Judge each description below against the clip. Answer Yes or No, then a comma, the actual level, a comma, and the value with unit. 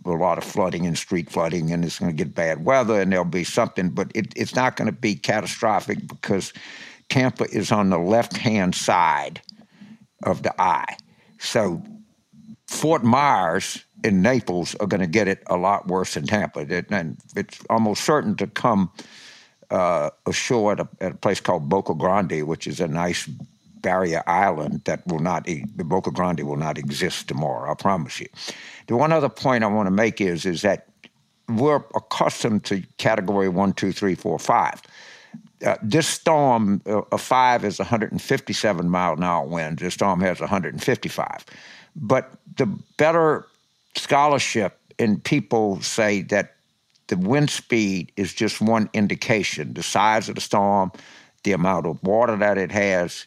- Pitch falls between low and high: No, low, 105 Hz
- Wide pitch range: Yes, wide, 7.6 semitones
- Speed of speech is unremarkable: Yes, average, 165 wpm